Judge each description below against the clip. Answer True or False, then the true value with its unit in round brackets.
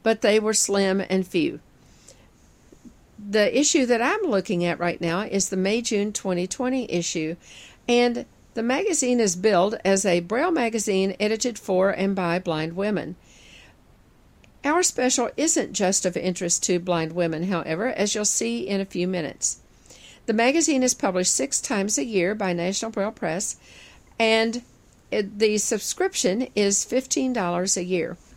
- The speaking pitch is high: True (200 Hz)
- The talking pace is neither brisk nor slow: True (150 wpm)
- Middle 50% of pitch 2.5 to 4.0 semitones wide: False (4.9 semitones)